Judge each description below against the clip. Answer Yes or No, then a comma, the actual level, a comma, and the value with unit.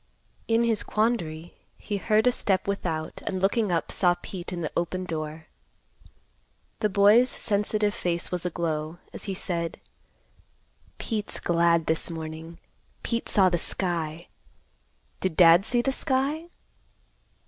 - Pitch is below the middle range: No, medium, 180 Hz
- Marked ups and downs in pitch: No, average, 4.2 semitones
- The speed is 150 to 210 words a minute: No, slow, 135 wpm